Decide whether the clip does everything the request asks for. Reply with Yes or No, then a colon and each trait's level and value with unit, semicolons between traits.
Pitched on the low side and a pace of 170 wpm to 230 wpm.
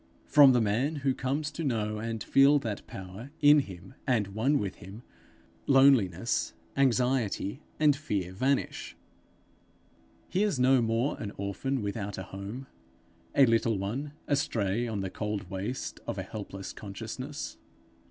No: low, 115 Hz; average, 145 wpm